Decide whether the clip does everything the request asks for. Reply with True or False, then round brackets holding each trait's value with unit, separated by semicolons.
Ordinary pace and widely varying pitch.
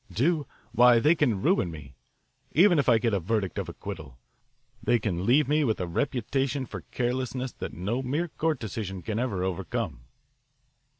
True (170 wpm; 5.8 semitones)